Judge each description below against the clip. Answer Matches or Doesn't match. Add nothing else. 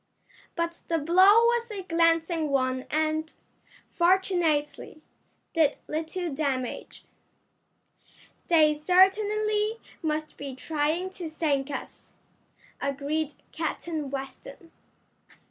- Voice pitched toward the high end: Matches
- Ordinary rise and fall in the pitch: Matches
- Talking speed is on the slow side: Matches